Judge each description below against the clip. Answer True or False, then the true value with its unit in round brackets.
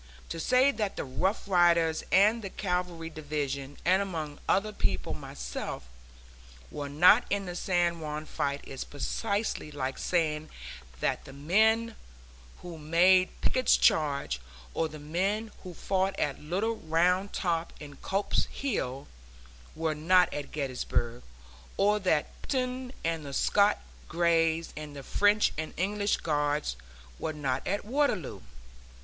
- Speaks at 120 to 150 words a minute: True (135 wpm)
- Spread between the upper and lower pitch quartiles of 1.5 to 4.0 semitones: False (4.9 semitones)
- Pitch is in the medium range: True (170 Hz)